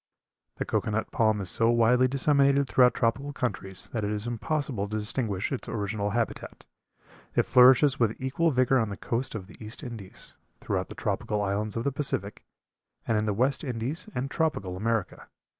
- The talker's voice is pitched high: No, low, 115 Hz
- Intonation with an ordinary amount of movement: Yes, average, 4.0 semitones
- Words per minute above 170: Yes, average, 180 wpm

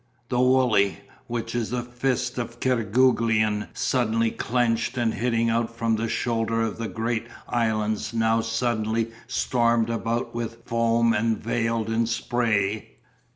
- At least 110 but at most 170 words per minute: Yes, slow, 135 wpm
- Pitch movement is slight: Yes, narrow, 1.0 semitones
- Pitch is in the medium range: No, low, 115 Hz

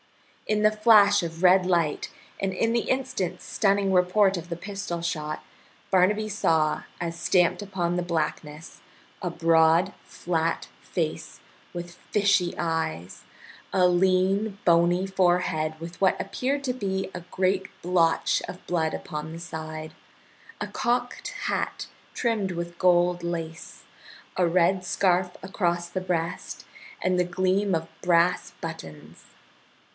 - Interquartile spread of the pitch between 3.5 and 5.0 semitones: No, narrow, 2.4 semitones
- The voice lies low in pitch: No, medium, 180 Hz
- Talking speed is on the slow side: Yes, slow, 130 wpm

